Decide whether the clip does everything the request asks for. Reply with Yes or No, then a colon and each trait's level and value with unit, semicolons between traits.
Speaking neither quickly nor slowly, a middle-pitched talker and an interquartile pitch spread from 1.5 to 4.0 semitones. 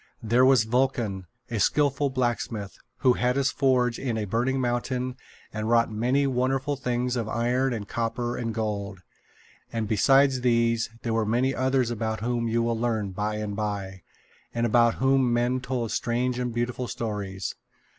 No: average, 165 wpm; low, 120 Hz; narrow, 2.4 semitones